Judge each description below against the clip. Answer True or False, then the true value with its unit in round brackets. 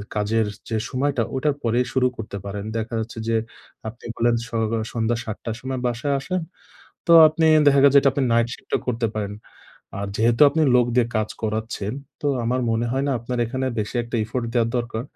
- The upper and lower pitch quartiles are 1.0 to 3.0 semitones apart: True (2.6 semitones)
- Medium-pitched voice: False (115 Hz)